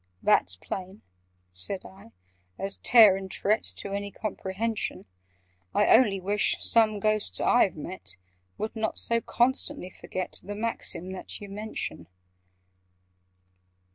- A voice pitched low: No, high, 200 Hz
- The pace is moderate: No, slow, 120 wpm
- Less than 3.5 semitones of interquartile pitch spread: Yes, narrow, 2.6 semitones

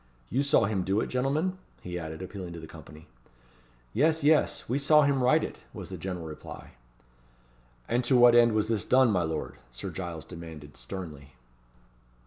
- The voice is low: Yes, low, 100 Hz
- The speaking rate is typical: Yes, average, 175 wpm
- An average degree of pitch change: No, wide, 7.8 semitones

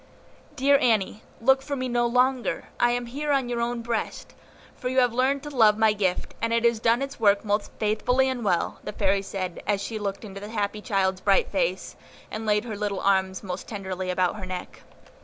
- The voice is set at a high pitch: Yes, high, 220 Hz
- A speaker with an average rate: No, fast, 215 wpm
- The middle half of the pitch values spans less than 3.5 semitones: No, average, 3.9 semitones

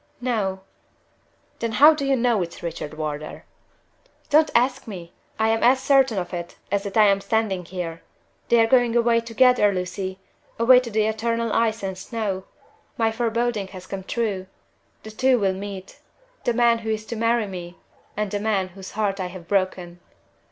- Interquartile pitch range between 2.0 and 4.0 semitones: Yes, average, 3.7 semitones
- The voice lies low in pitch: No, high, 215 Hz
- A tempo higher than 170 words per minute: Yes, average, 180 wpm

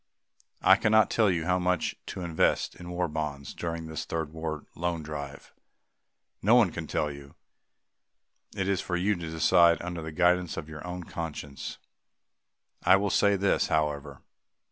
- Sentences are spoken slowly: No, average, 165 wpm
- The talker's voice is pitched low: Yes, very low, 85 Hz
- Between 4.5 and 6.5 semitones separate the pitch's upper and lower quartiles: No, average, 2.8 semitones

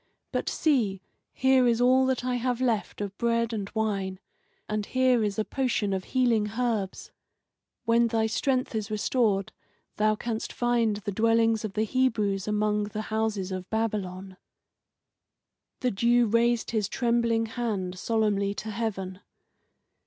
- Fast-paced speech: No, average, 145 wpm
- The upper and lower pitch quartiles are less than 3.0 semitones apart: Yes, narrow, 2.6 semitones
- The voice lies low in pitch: No, high, 220 Hz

